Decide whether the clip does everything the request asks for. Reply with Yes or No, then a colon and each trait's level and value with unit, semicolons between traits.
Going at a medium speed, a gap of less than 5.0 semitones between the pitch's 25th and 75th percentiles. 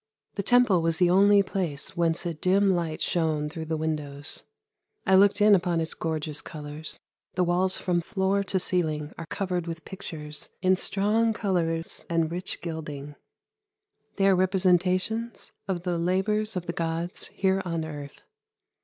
Yes: average, 155 wpm; average, 3.0 semitones